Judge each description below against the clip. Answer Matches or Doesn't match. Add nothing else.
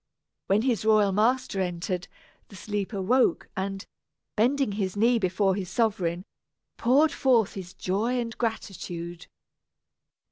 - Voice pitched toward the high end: Matches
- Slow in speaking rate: Matches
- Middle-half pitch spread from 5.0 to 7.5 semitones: Doesn't match